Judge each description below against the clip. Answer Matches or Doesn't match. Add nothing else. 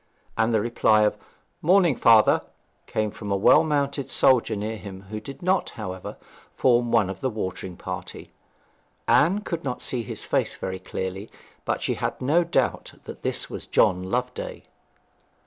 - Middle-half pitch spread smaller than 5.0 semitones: Doesn't match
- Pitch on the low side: Matches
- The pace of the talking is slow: Doesn't match